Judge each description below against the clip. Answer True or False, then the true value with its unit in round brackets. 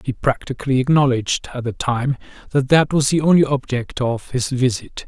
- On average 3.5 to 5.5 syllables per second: True (5.3 syllables/s)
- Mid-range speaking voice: False (130 Hz)